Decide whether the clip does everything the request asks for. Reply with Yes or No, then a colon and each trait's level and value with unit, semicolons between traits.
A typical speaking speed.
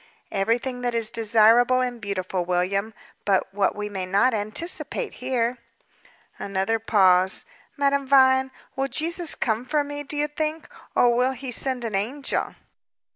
Yes: average, 145 wpm